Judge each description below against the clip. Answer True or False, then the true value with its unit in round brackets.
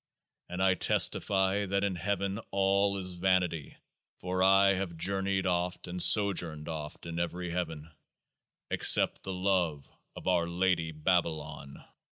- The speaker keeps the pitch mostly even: True (2.3 semitones)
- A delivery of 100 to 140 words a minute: True (135 wpm)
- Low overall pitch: True (90 Hz)